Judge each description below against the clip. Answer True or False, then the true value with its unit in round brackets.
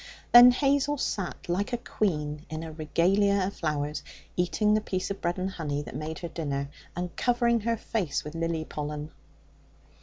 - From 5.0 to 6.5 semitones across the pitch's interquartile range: True (5.6 semitones)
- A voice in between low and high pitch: True (175 Hz)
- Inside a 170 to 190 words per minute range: True (175 wpm)